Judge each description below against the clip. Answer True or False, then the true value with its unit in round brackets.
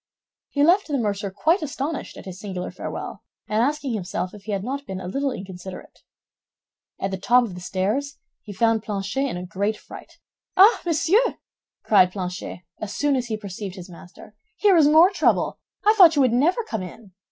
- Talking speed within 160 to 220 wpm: True (195 wpm)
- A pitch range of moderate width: False (7.2 semitones)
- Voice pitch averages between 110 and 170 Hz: False (220 Hz)